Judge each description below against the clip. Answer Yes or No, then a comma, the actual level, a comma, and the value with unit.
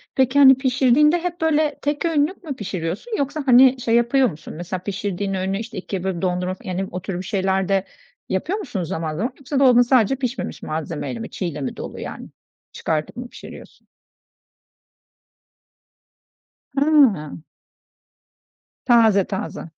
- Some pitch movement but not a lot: No, wide, 6.4 semitones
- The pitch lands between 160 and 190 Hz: No, high, 225 Hz